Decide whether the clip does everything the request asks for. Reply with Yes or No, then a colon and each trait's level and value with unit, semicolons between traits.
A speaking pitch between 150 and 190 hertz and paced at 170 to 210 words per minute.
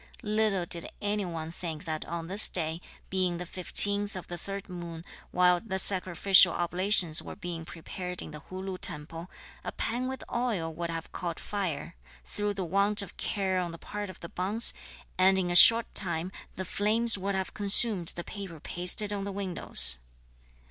Yes: medium, 185 Hz; average, 185 wpm